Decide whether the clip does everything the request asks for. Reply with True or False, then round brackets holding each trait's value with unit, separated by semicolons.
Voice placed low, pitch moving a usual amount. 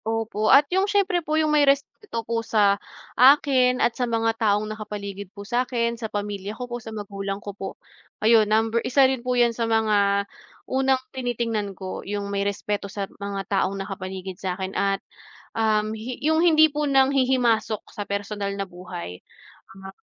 False (220 Hz; 3.8 semitones)